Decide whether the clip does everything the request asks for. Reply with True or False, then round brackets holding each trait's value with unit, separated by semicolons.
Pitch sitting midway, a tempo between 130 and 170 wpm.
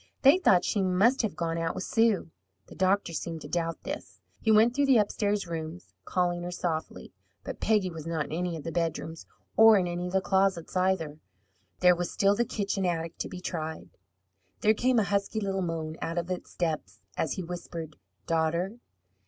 False (180 Hz; 195 wpm)